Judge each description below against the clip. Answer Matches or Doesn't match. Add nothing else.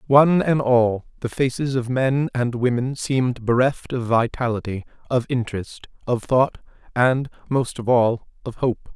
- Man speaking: Matches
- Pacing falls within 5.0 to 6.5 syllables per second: Doesn't match